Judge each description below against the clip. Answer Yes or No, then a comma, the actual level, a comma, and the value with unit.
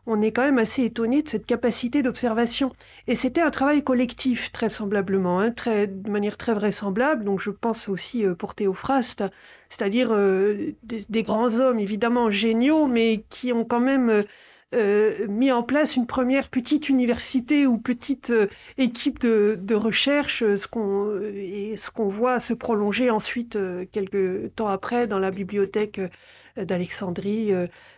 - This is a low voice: No, high, 225 Hz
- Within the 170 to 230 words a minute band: No, average, 155 wpm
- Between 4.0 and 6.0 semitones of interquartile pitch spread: No, average, 3.4 semitones